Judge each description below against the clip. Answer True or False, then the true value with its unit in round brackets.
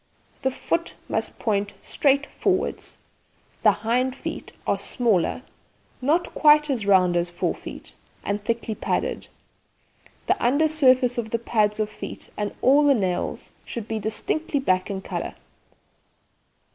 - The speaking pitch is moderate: False (235 Hz)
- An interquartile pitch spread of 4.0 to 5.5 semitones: True (5.2 semitones)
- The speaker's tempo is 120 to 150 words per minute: True (140 wpm)